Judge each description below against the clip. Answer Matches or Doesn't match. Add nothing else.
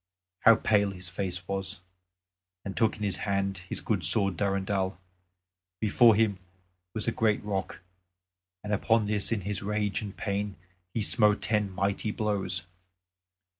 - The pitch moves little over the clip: Matches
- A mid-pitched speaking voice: Doesn't match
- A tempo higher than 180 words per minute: Doesn't match